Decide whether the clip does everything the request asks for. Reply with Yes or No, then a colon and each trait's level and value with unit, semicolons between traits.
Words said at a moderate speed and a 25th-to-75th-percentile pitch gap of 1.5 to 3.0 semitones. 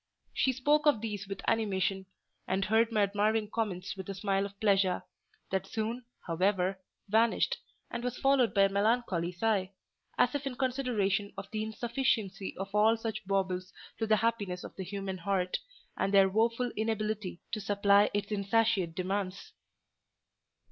Yes: average, 155 wpm; average, 2.7 semitones